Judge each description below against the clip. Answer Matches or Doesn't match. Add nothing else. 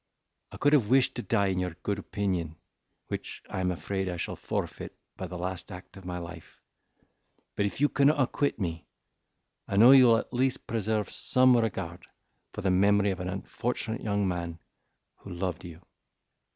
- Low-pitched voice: Matches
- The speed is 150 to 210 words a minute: Matches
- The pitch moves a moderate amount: Matches